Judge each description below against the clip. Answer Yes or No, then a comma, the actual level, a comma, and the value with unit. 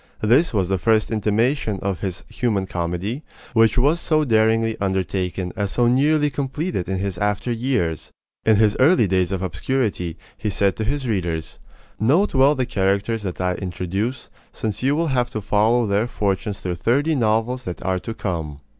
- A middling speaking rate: Yes, average, 175 wpm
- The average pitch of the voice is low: Yes, low, 110 Hz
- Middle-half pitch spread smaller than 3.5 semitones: No, average, 4.7 semitones